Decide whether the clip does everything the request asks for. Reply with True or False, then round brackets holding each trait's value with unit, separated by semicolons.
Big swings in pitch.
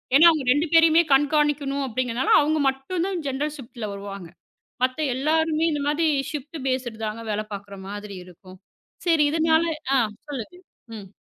True (5.7 semitones)